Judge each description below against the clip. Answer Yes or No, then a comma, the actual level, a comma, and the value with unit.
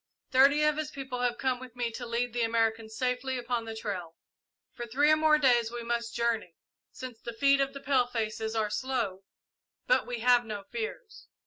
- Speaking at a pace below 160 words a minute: No, average, 195 wpm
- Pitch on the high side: Yes, high, 245 Hz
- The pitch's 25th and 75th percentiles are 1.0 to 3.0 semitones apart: Yes, average, 2.7 semitones